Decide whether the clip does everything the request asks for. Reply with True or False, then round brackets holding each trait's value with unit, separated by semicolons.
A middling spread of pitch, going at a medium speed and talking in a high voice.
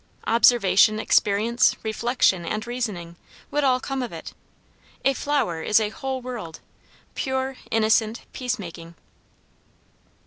False (4.1 semitones; 110 wpm; 230 Hz)